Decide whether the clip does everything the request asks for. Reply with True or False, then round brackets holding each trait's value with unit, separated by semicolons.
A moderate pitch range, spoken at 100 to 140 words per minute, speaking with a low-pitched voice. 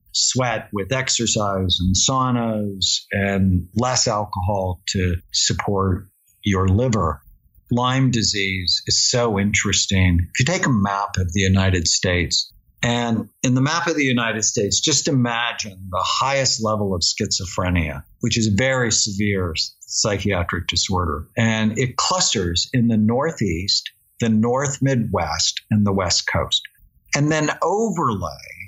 True (4.2 semitones; 135 wpm; 105 Hz)